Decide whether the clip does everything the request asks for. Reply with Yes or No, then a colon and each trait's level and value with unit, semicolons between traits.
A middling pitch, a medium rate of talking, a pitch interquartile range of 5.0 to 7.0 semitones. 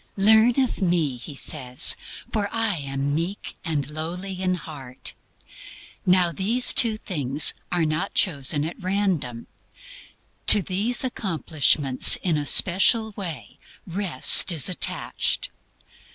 No: medium, 175 Hz; slow, 120 wpm; average, 5.3 semitones